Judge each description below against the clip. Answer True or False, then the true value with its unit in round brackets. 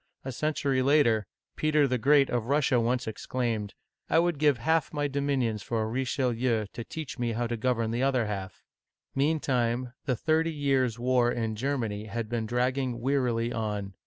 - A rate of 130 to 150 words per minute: False (180 wpm)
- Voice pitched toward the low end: True (125 Hz)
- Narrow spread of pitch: False (3.4 semitones)